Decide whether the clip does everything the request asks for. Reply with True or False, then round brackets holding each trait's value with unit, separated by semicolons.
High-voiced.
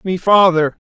False (175 Hz)